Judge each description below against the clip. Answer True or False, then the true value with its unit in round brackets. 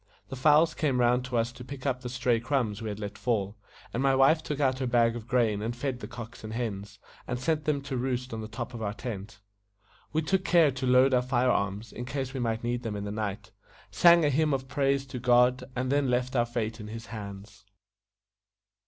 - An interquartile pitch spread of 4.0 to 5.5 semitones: False (3.0 semitones)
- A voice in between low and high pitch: False (125 Hz)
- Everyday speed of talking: False (230 wpm)